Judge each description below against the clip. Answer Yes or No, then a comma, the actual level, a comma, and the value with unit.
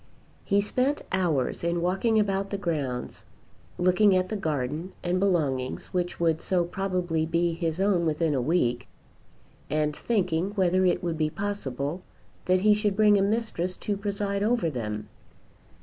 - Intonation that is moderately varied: Yes, average, 3.9 semitones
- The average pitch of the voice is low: No, medium, 180 Hz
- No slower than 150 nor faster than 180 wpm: Yes, average, 155 wpm